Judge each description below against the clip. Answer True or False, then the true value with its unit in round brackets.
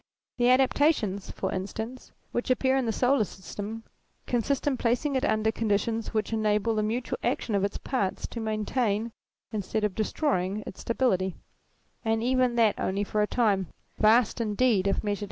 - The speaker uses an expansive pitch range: False (3.2 semitones)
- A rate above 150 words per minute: True (165 wpm)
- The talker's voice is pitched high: True (220 Hz)